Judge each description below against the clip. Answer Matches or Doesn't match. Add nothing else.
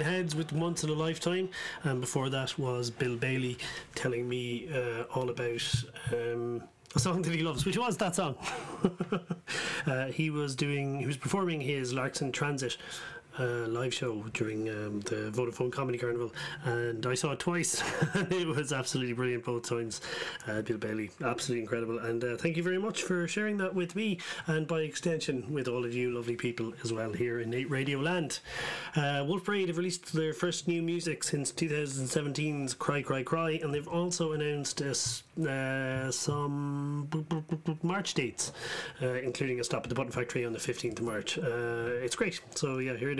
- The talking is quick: Doesn't match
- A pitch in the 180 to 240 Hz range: Doesn't match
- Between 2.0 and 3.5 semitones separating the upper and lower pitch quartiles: Doesn't match